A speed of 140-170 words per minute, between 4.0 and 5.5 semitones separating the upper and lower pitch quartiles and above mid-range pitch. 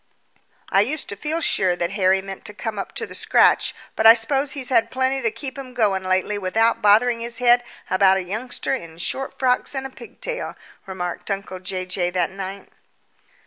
No: average, 195 wpm; average, 4.9 semitones; high, 210 Hz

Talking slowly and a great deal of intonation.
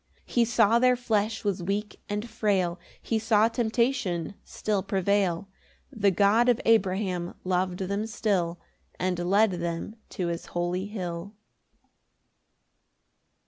No: slow, 125 wpm; average, 3.5 semitones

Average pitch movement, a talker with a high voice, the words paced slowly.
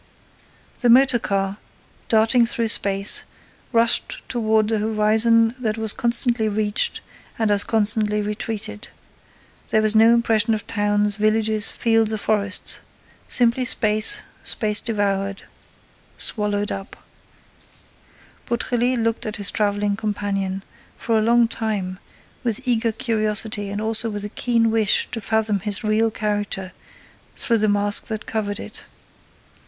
No: narrow, 1.6 semitones; high, 215 Hz; slow, 130 wpm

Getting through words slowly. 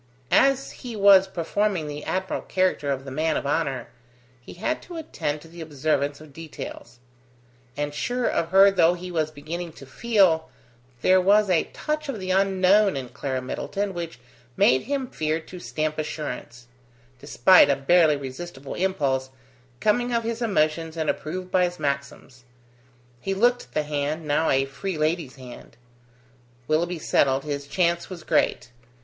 No: average, 160 wpm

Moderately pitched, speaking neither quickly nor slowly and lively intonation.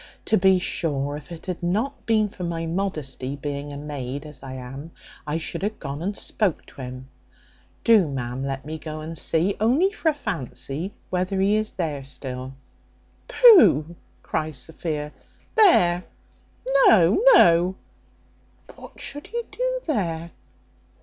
Yes: medium, 165 Hz; average, 150 wpm; wide, 5.9 semitones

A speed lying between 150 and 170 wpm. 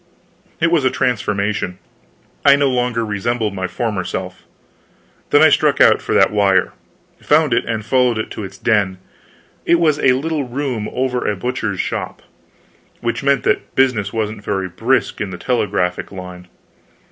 Yes: average, 160 wpm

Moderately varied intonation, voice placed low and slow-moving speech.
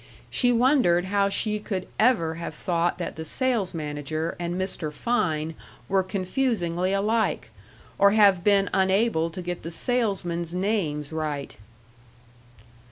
No: average, 4.0 semitones; medium, 185 Hz; slow, 130 wpm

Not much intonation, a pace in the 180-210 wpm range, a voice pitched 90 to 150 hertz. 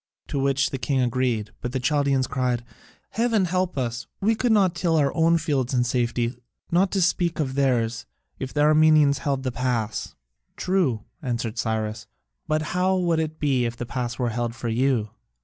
No: average, 4.9 semitones; average, 185 wpm; low, 135 Hz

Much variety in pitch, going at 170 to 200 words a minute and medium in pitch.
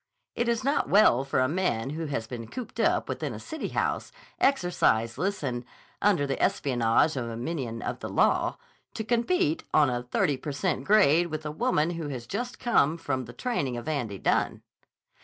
Yes: wide, 8.5 semitones; average, 190 wpm; medium, 150 Hz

